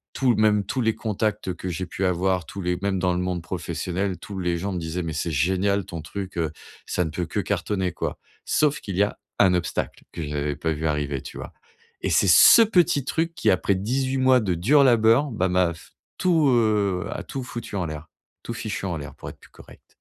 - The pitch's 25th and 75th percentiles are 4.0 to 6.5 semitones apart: Yes, average, 4.5 semitones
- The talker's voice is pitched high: No, very low, 95 Hz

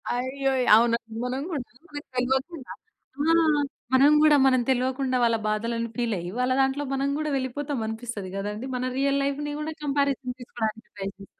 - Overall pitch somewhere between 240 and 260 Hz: Yes, very high, 255 Hz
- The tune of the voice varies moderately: Yes, average, 3.1 semitones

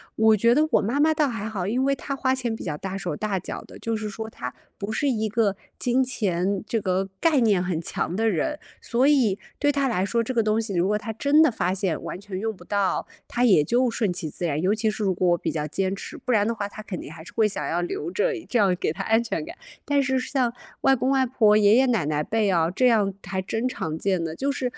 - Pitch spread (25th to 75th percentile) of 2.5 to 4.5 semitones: No, average, 4.9 semitones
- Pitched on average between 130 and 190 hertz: No, high, 215 Hz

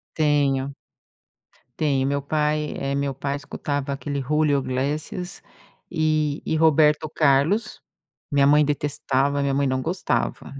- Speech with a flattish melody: Yes, narrow, 1.7 semitones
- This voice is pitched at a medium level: Yes, medium, 145 Hz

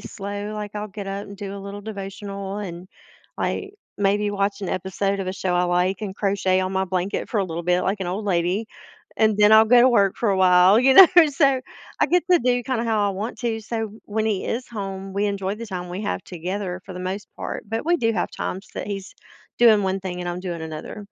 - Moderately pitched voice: No, high, 200 Hz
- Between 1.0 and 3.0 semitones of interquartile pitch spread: Yes, narrow, 2.5 semitones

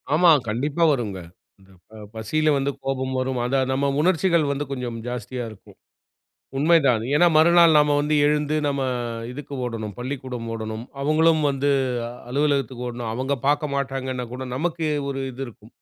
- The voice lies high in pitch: No, low, 135 Hz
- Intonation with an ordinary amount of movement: Yes, average, 3.4 semitones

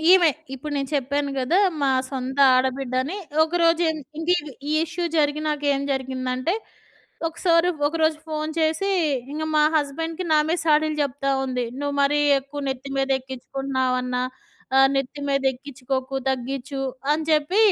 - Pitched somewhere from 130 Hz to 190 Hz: No, very high, 285 Hz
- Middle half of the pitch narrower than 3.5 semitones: Yes, average, 2.9 semitones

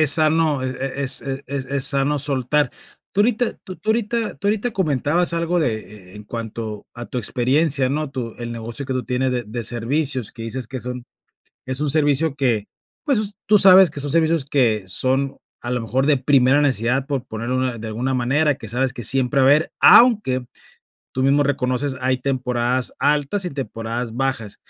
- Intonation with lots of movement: No, average, 3.3 semitones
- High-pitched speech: No, low, 135 Hz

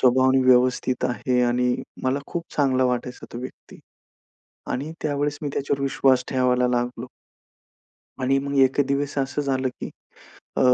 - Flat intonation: Yes, narrow, 1.8 semitones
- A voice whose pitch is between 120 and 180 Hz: Yes, low, 130 Hz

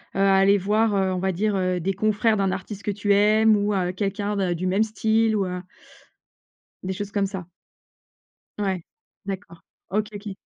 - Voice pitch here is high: Yes, high, 200 Hz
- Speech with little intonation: Yes, narrow, 1.8 semitones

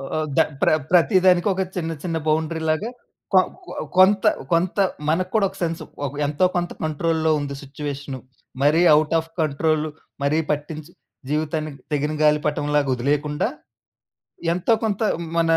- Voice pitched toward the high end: No, medium, 155 Hz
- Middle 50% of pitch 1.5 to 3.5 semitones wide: Yes, average, 2.8 semitones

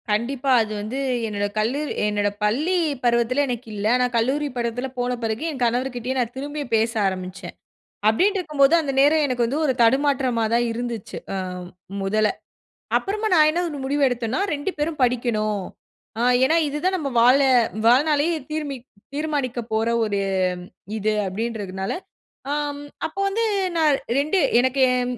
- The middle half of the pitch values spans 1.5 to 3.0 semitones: No, average, 4.4 semitones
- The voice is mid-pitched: No, very high, 250 Hz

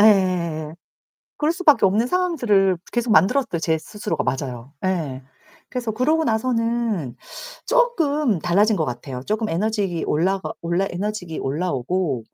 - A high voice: Yes, high, 195 Hz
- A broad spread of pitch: Yes, wide, 6.3 semitones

